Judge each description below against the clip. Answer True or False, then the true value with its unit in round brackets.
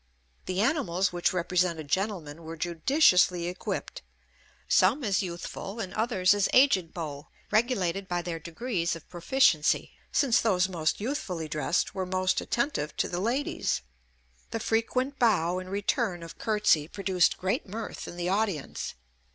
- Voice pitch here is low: False (185 Hz)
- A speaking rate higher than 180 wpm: False (145 wpm)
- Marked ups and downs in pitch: False (4.4 semitones)